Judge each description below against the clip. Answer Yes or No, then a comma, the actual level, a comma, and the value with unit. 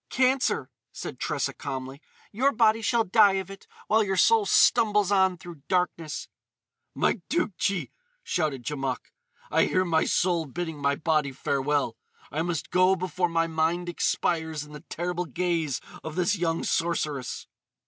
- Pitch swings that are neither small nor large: Yes, average, 4.0 semitones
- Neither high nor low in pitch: Yes, medium, 175 Hz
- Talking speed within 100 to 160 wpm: Yes, average, 150 wpm